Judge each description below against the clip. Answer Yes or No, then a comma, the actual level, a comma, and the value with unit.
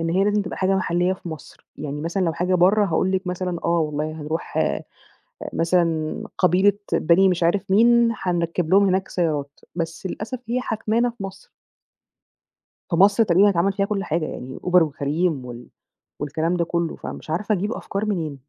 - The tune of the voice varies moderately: Yes, average, 3.3 semitones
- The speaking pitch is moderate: Yes, medium, 180 Hz